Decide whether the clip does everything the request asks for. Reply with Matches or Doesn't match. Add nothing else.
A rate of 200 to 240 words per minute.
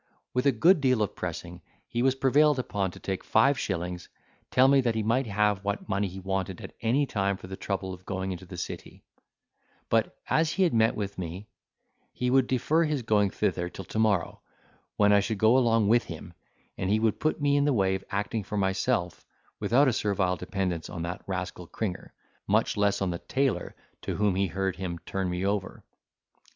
Matches